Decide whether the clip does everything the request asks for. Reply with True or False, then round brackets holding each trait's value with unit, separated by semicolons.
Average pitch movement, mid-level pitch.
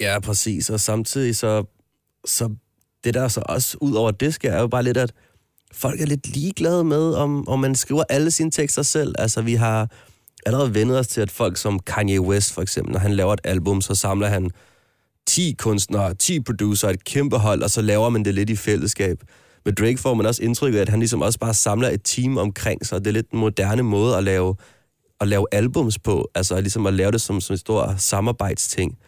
False (3.9 semitones; 110 Hz)